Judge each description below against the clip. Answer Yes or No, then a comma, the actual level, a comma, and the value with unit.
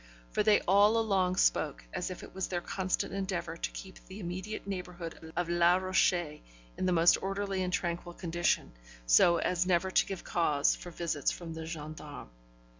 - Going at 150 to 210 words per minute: Yes, average, 180 wpm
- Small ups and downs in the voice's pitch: Yes, narrow, 2.0 semitones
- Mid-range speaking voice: Yes, medium, 180 Hz